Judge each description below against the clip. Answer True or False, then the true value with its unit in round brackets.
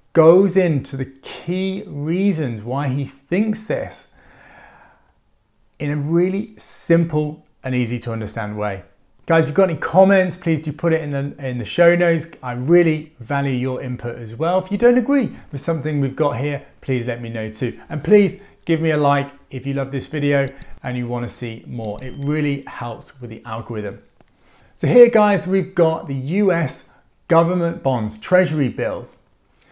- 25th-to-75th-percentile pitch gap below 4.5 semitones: False (5.1 semitones)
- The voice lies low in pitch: False (145 Hz)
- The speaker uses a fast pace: False (180 wpm)